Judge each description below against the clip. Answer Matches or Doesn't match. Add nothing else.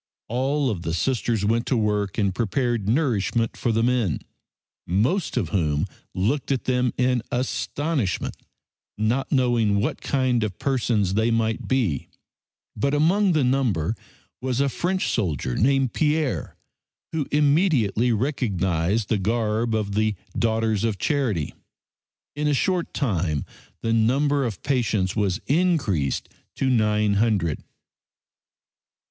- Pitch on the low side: Matches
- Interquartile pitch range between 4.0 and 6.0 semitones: Matches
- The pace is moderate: Doesn't match